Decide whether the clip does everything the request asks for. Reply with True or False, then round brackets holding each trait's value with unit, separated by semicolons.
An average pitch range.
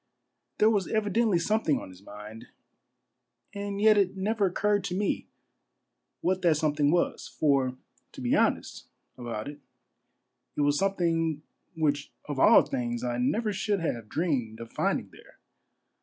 False (7.5 semitones)